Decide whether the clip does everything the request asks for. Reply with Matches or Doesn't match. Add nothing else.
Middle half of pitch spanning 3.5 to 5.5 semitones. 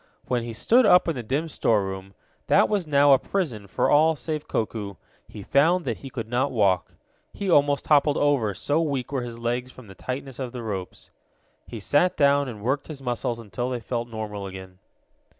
Matches